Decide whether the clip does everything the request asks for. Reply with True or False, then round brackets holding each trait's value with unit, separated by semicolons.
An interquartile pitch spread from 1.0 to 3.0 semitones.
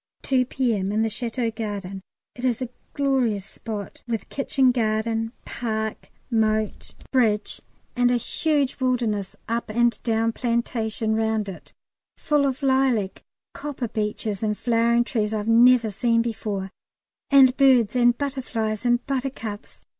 True (2.7 semitones)